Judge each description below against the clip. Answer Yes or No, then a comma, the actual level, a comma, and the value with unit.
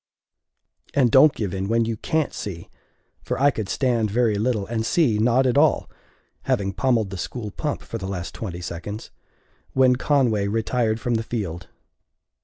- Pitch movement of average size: Yes, average, 3.9 semitones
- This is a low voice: Yes, low, 115 Hz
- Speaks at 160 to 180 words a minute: Yes, average, 170 wpm